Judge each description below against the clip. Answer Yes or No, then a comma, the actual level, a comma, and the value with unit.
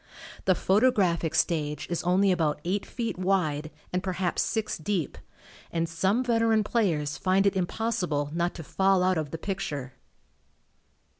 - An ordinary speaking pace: Yes, average, 145 wpm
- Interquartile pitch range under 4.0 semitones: Yes, average, 3.5 semitones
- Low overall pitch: No, medium, 180 Hz